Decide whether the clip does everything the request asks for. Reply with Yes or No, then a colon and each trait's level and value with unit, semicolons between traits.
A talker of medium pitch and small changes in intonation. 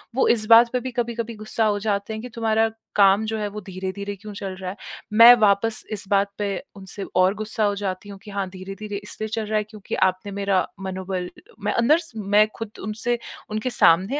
No: high, 210 Hz; narrow, 2.0 semitones